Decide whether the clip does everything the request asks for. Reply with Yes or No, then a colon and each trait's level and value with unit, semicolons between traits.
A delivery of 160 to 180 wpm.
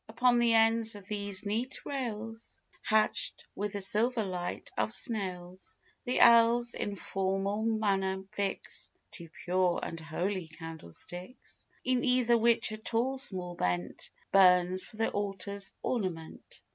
No: slow, 135 wpm